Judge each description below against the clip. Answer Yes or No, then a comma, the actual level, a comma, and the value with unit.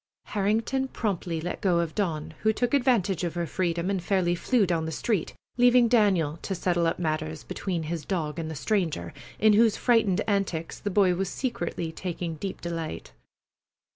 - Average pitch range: Yes, average, 4.2 semitones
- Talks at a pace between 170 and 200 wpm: Yes, average, 175 wpm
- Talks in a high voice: No, medium, 180 Hz